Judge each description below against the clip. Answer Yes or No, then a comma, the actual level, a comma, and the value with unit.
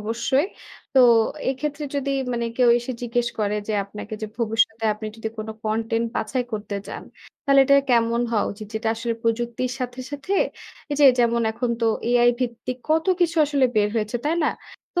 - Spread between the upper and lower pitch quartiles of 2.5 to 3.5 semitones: Yes, average, 2.8 semitones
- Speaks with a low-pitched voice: No, high, 235 Hz